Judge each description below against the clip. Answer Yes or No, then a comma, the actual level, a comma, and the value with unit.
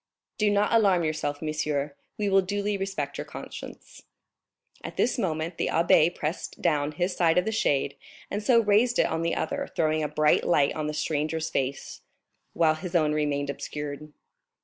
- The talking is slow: No, average, 175 wpm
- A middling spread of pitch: Yes, average, 4.4 semitones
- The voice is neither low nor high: Yes, medium, 160 Hz